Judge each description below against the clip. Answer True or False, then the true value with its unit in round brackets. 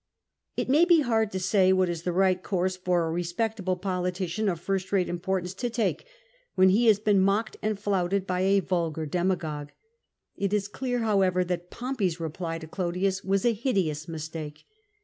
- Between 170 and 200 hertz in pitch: True (185 Hz)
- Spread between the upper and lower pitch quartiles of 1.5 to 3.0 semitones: True (2.7 semitones)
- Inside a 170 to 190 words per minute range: True (185 wpm)